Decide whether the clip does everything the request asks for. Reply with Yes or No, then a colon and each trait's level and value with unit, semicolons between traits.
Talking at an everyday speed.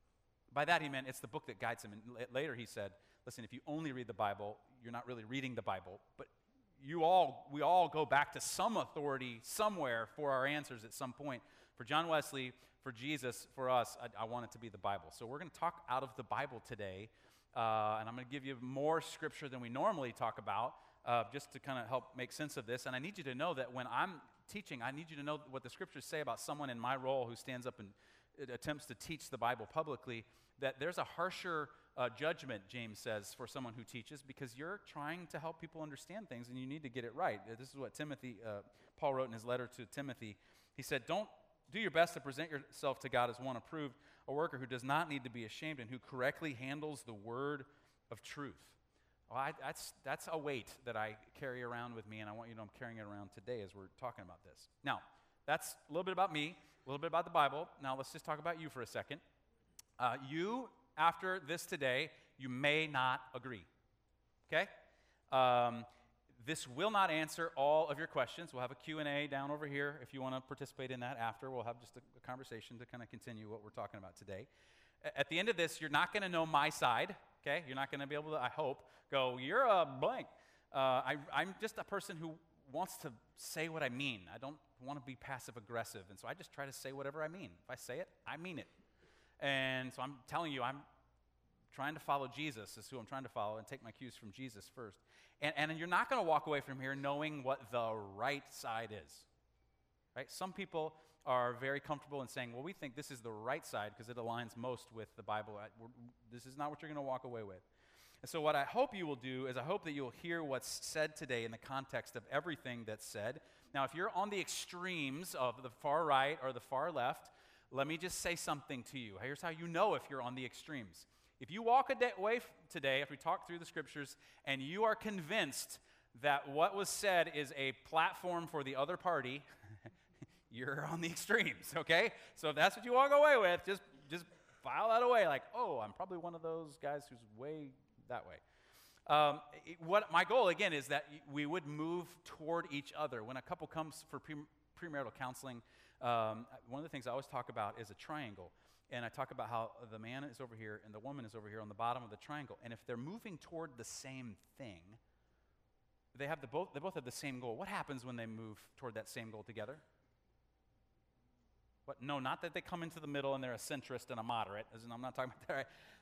No: fast, 235 wpm